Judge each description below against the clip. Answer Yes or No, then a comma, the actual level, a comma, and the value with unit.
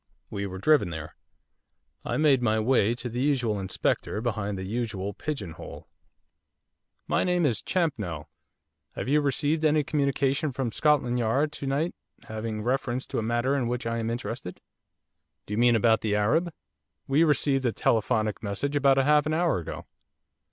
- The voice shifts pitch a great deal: No, average, 4.9 semitones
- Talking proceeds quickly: No, average, 165 wpm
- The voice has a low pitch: Yes, low, 125 Hz